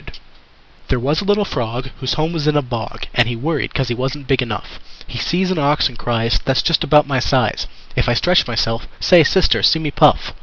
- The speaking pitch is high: No, low, 135 Hz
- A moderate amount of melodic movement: Yes, average, 4.6 semitones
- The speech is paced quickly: Yes, fast, 225 wpm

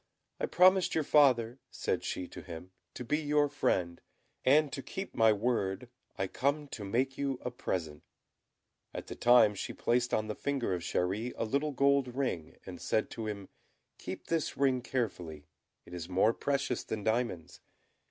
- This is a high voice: No, low, 120 Hz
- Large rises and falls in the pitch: Yes, wide, 6.4 semitones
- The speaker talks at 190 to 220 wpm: No, average, 175 wpm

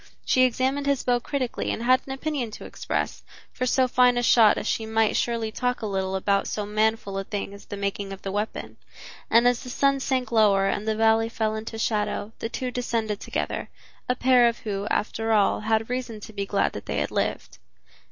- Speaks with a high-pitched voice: Yes, high, 225 Hz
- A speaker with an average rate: No, fast, 210 wpm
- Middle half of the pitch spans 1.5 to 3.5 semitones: Yes, average, 3.0 semitones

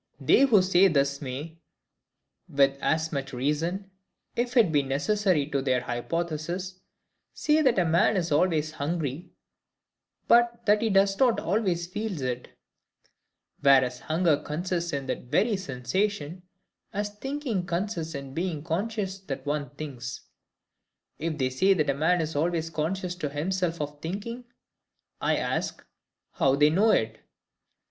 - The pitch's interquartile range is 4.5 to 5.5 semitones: Yes, average, 5.2 semitones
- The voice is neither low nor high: Yes, medium, 165 Hz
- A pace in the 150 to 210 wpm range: No, average, 140 wpm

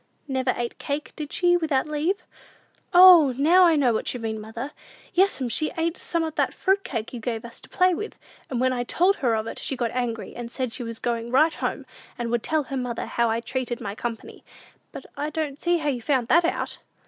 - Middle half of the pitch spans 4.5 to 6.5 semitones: Yes, average, 5.3 semitones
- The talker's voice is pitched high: Yes, very high, 260 Hz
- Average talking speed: No, fast, 230 wpm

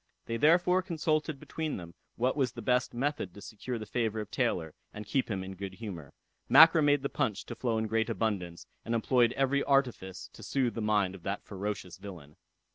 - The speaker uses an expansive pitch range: Yes, wide, 5.7 semitones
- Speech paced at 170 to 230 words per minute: Yes, average, 200 wpm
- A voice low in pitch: Yes, low, 115 Hz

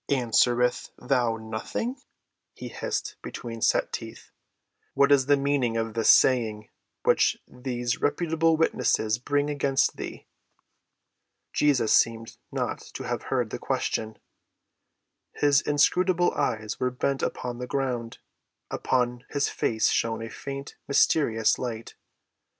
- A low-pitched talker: Yes, low, 125 Hz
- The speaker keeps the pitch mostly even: No, average, 3.9 semitones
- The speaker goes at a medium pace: No, slow, 120 wpm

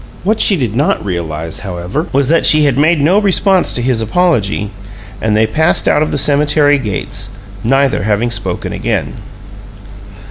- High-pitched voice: No, low, 135 Hz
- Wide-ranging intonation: Yes, wide, 6.5 semitones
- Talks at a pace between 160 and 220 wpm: Yes, average, 165 wpm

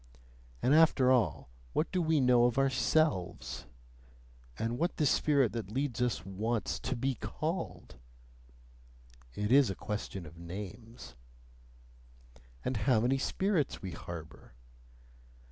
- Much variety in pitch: Yes, wide, 5.9 semitones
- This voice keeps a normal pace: No, slow, 125 wpm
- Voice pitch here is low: Yes, low, 120 Hz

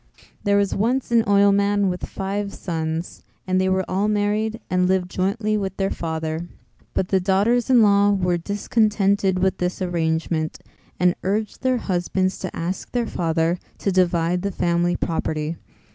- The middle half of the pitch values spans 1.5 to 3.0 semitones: Yes, narrow, 2.5 semitones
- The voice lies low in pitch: No, high, 190 Hz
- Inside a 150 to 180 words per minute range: Yes, average, 160 wpm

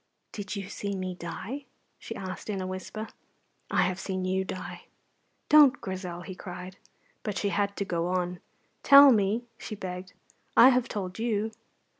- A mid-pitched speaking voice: No, high, 195 Hz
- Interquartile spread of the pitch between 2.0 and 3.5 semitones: Yes, average, 2.7 semitones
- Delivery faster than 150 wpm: Yes, average, 165 wpm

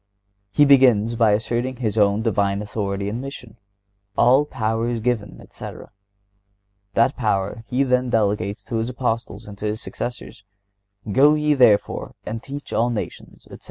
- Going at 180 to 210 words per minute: No, average, 160 wpm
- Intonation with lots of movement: No, average, 3.3 semitones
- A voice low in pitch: Yes, low, 115 Hz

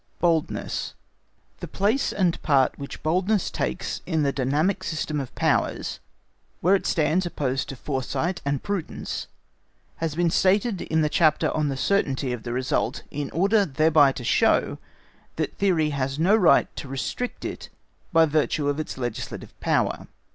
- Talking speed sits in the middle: Yes, average, 155 wpm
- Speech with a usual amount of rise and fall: Yes, average, 4.6 semitones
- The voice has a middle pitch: Yes, medium, 155 Hz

